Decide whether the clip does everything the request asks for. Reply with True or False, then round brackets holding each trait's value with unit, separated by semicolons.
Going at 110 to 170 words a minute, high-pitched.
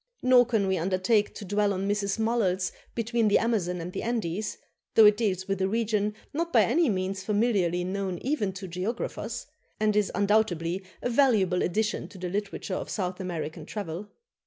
False (180 wpm; 200 Hz)